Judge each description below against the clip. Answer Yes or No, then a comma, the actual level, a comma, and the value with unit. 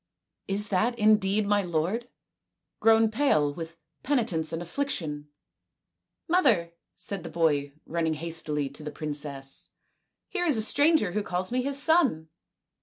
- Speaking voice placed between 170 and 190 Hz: Yes, medium, 185 Hz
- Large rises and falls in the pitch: Yes, wide, 6.6 semitones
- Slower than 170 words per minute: Yes, average, 155 wpm